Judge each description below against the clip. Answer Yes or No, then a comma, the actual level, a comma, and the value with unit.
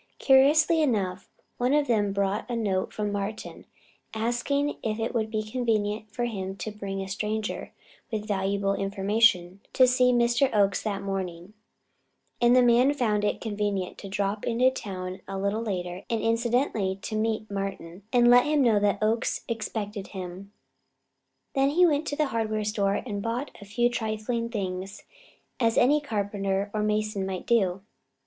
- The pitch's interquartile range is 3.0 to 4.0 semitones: Yes, average, 3.3 semitones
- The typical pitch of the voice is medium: No, high, 215 Hz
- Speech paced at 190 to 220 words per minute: No, average, 165 wpm